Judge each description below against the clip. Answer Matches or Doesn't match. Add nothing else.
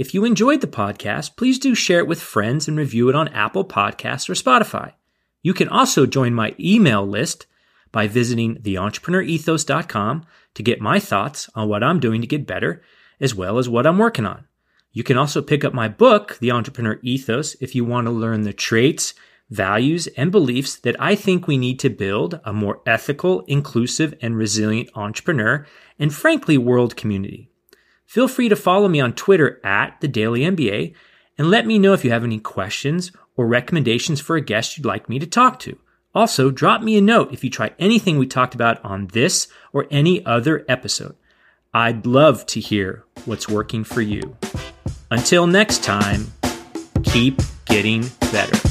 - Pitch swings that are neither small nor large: Doesn't match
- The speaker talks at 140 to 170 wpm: Doesn't match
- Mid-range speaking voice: Doesn't match